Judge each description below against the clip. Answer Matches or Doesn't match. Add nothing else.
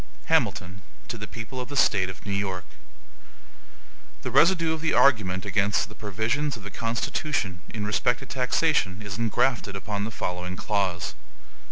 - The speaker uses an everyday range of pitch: Matches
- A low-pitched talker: Matches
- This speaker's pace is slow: Doesn't match